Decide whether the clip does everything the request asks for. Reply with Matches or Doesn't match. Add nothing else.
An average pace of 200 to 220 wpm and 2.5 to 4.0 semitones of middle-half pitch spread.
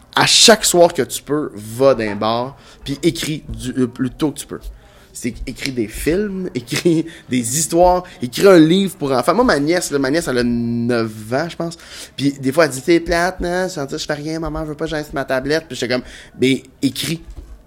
Doesn't match